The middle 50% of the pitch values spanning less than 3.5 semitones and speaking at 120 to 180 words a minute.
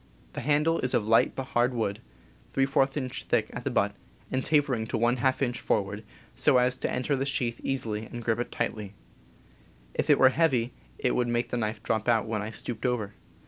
No: average, 2.9 semitones; fast, 205 wpm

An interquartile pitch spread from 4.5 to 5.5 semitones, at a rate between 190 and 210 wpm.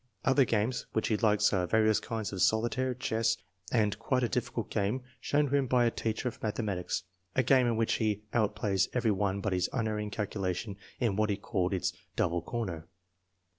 No: average, 3.0 semitones; average, 195 wpm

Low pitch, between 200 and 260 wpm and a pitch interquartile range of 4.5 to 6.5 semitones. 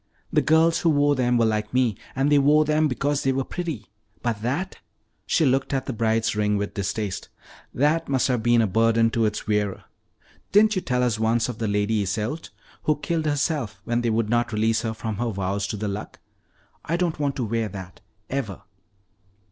Yes: low, 120 Hz; fast, 205 wpm; average, 5.0 semitones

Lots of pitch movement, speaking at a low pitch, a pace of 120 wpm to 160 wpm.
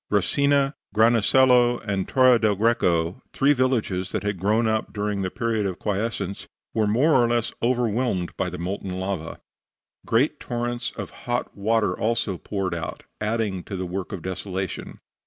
No: average, 4.0 semitones; low, 105 Hz; average, 155 wpm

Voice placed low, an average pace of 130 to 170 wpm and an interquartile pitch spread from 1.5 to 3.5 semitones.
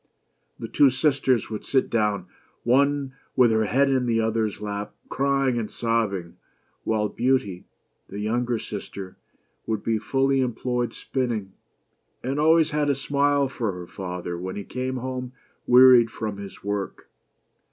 No: low, 120 Hz; average, 150 wpm; average, 4.2 semitones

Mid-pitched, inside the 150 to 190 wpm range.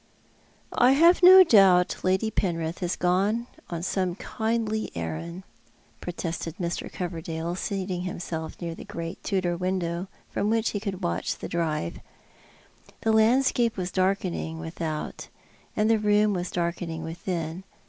No: medium, 180 Hz; average, 140 wpm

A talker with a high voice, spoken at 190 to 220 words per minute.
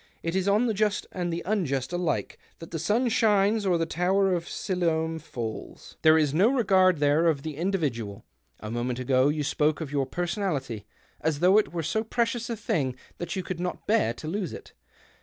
No: medium, 170 Hz; average, 200 wpm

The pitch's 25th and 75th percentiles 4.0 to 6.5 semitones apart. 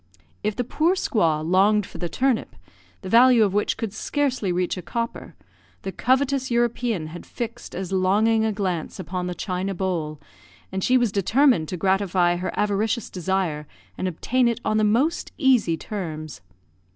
Yes: average, 4.7 semitones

